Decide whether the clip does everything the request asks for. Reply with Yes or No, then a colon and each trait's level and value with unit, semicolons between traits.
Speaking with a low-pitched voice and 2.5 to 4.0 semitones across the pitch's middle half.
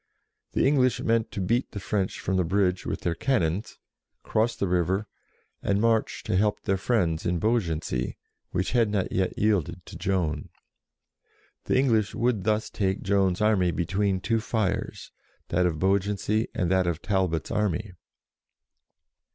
Yes: low, 100 Hz; average, 3.1 semitones